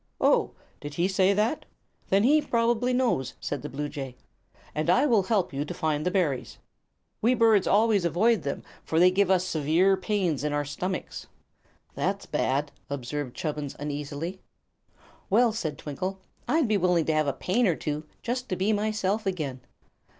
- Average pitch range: No, wide, 6.4 semitones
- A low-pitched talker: No, medium, 180 Hz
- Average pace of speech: Yes, average, 170 wpm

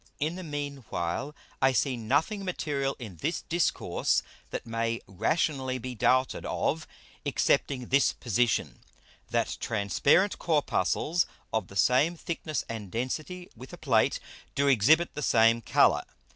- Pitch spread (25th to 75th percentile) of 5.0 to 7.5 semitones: Yes, average, 5.3 semitones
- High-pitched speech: No, low, 135 Hz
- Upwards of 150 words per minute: No, slow, 135 wpm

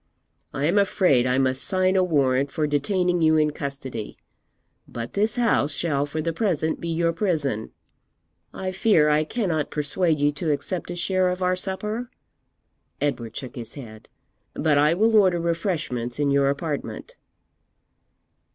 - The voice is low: No, medium, 155 Hz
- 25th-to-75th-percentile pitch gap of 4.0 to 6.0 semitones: Yes, average, 4.6 semitones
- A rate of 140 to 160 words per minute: Yes, average, 155 wpm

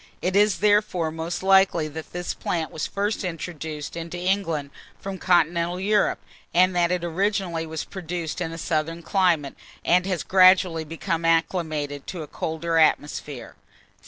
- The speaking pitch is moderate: Yes, medium, 170 Hz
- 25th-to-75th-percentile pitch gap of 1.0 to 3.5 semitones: Yes, narrow, 2.5 semitones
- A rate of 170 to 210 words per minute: No, average, 150 wpm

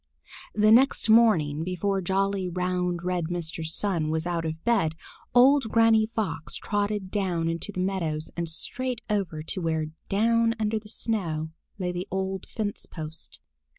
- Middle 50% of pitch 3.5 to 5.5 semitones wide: Yes, average, 4.5 semitones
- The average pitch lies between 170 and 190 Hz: Yes, medium, 185 Hz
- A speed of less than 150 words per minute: No, average, 155 wpm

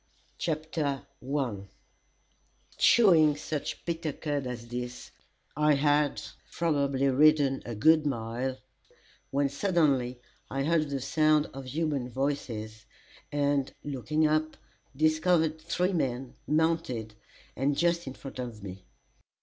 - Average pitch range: Yes, average, 3.5 semitones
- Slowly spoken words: Yes, slow, 115 wpm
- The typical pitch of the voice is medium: Yes, medium, 145 Hz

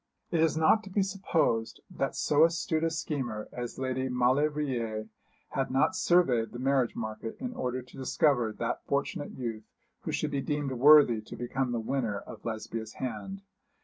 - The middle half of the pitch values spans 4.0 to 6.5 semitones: Yes, average, 4.6 semitones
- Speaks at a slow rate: No, average, 170 wpm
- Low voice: Yes, low, 130 Hz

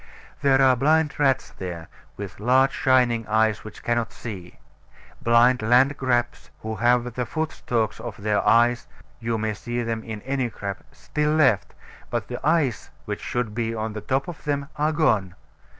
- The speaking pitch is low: Yes, low, 120 Hz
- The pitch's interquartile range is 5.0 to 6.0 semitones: No, average, 3.5 semitones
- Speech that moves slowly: No, average, 165 wpm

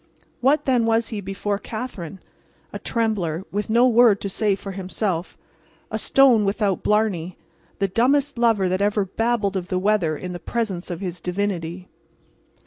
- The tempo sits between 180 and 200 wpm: No, average, 160 wpm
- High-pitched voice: Yes, high, 200 Hz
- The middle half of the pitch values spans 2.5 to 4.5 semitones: Yes, average, 3.7 semitones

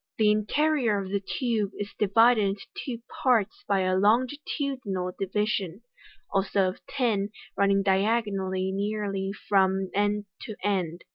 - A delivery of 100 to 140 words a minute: Yes, slow, 135 wpm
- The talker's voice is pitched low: No, high, 205 Hz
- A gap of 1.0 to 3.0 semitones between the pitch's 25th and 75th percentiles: Yes, narrow, 2.6 semitones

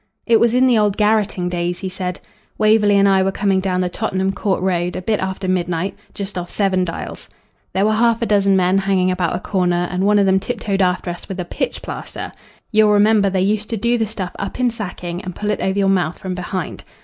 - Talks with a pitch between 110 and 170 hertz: No, high, 195 Hz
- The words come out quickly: Yes, fast, 235 wpm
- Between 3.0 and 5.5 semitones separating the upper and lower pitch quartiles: No, narrow, 2.4 semitones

